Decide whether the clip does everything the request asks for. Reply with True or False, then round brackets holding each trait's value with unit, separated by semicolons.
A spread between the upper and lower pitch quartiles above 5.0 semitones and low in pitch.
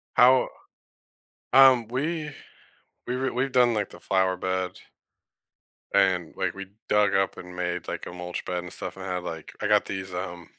True (5.5 semitones; 95 Hz)